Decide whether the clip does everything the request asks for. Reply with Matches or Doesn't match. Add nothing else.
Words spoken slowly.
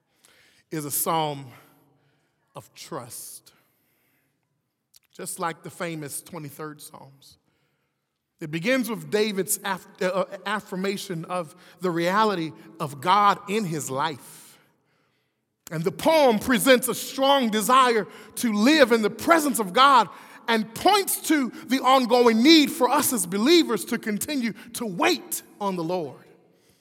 Matches